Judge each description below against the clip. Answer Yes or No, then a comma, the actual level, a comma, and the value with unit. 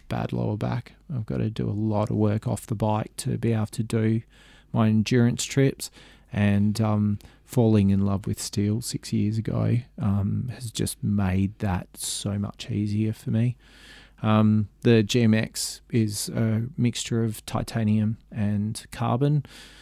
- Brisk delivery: No, average, 155 wpm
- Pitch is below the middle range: Yes, low, 110 Hz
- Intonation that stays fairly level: Yes, narrow, 2.0 semitones